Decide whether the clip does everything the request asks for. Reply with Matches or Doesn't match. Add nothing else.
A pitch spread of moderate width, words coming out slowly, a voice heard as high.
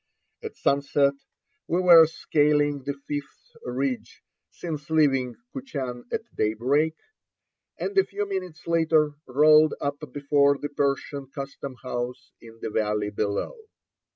Doesn't match